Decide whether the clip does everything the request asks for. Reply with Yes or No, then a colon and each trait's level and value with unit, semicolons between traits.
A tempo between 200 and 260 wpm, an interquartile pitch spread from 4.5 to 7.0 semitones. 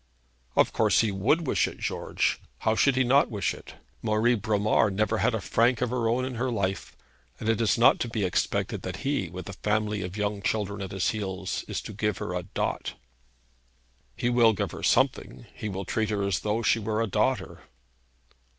No: fast, 205 wpm; average, 2.8 semitones